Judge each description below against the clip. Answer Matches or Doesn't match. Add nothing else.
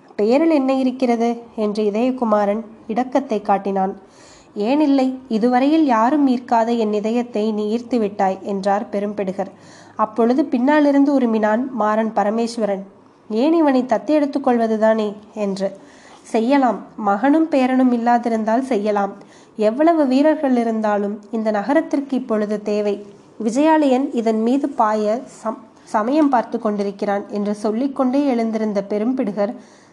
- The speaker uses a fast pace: Doesn't match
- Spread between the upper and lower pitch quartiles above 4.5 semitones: Doesn't match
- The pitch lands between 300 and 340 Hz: Doesn't match